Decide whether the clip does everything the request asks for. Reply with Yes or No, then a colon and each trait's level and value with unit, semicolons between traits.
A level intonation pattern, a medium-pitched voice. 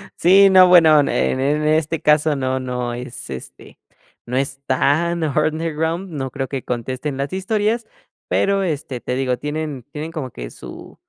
No: average, 4.0 semitones; medium, 150 Hz